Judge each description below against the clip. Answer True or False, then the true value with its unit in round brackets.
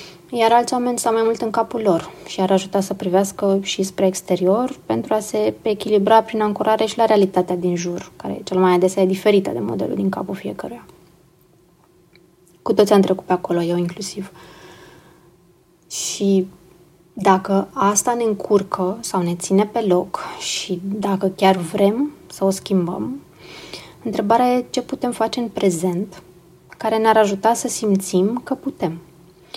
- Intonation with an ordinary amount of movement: True (3.4 semitones)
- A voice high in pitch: True (195 Hz)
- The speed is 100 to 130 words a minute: False (160 wpm)